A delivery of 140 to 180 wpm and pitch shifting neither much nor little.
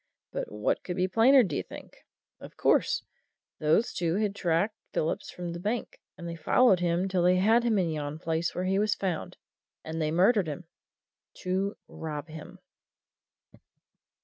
Yes: average, 165 wpm; average, 3.7 semitones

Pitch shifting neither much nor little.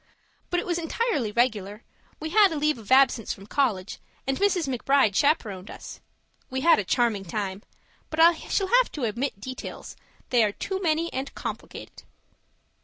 No: wide, 7.3 semitones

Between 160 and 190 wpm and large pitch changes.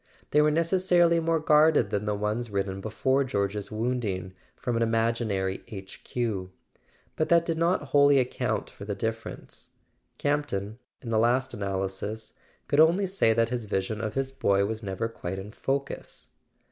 Yes: average, 165 wpm; wide, 6.0 semitones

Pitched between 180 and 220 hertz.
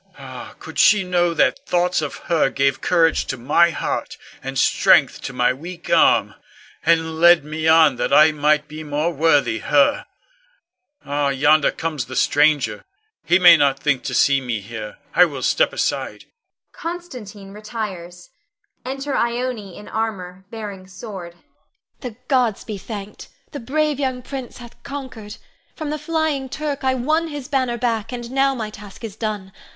Yes: high, 190 Hz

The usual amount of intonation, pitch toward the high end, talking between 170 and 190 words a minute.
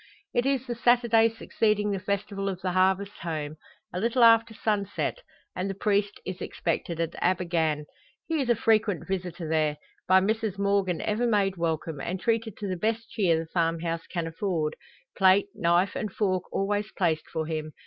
Yes: average, 4.1 semitones; high, 195 Hz; average, 180 wpm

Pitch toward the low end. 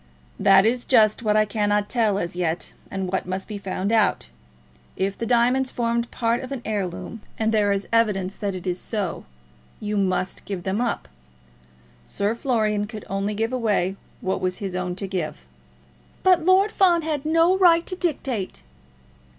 No: high, 210 Hz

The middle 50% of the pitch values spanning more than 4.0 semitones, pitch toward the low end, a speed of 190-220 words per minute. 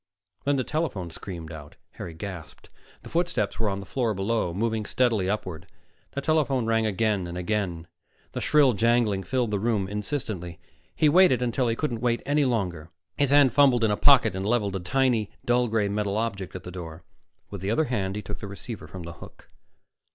Yes: average, 4.6 semitones; low, 110 Hz; average, 195 wpm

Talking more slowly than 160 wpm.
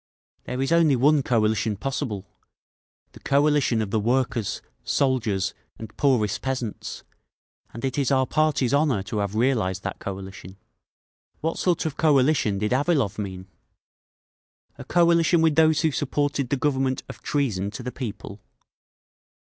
Yes: average, 140 wpm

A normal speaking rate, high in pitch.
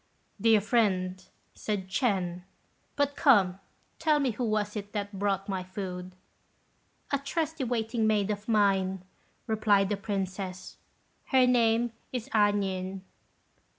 No: slow, 125 wpm; high, 205 Hz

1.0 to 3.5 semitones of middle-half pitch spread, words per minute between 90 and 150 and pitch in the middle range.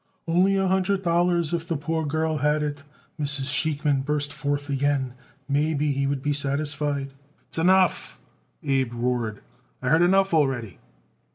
Yes: average, 2.8 semitones; average, 145 wpm; medium, 145 Hz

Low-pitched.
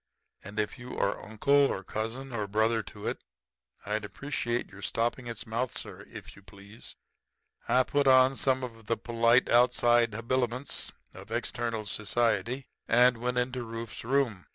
Yes: low, 120 Hz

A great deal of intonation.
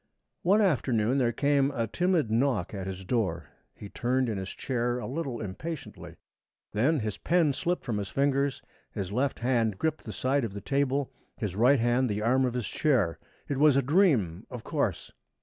No: average, 4.7 semitones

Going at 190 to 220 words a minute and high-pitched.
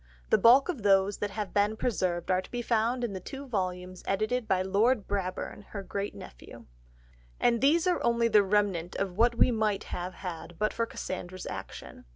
Yes: average, 195 wpm; high, 205 Hz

